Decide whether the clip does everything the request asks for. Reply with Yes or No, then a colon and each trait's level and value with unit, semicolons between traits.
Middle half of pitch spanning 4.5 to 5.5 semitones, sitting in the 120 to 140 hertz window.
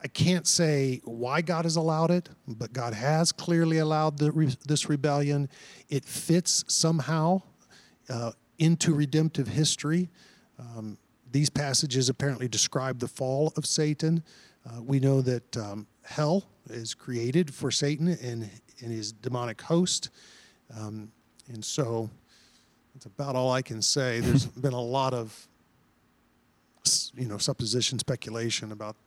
Yes: average, 4.9 semitones; low, 135 Hz